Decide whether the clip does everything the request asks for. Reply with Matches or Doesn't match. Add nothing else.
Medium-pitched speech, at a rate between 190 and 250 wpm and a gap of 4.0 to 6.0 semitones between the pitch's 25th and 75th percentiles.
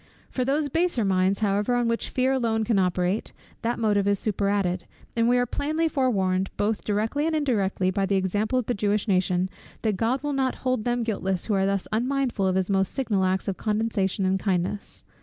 Doesn't match